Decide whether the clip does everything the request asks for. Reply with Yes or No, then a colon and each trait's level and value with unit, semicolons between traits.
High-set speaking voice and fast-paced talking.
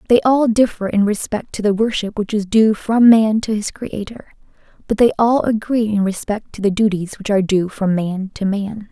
Yes: high, 210 Hz; fast, 215 wpm